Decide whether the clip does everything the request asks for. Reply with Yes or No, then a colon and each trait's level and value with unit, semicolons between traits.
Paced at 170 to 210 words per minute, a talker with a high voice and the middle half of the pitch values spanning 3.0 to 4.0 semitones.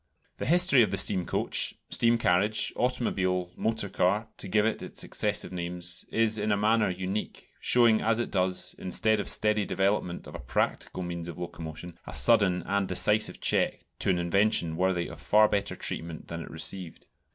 No: average, 180 wpm; very low, 95 Hz; average, 3.4 semitones